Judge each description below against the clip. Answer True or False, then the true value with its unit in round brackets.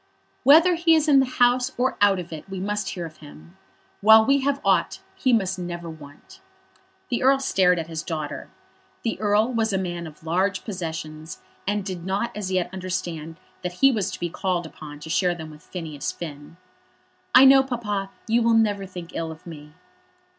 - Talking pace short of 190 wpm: False (195 wpm)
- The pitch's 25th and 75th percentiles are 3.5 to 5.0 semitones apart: False (5.6 semitones)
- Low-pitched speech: False (185 Hz)